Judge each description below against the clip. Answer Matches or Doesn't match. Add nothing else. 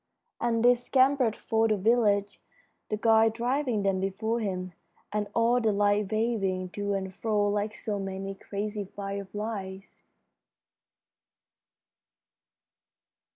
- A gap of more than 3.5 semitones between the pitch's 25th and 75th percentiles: Doesn't match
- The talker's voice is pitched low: Doesn't match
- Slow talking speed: Matches